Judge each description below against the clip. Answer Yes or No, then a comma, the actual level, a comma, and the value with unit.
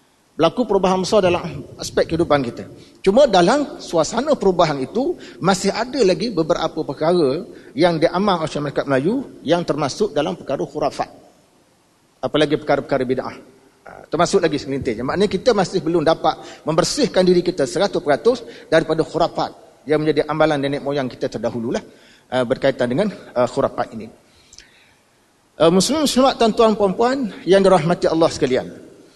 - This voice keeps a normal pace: Yes, average, 130 wpm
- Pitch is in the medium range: Yes, medium, 170 Hz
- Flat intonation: No, average, 5.3 semitones